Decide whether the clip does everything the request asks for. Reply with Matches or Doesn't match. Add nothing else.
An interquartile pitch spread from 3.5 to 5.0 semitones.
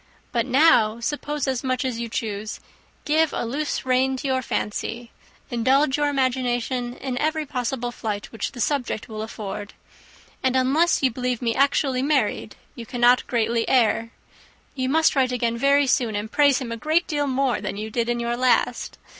Doesn't match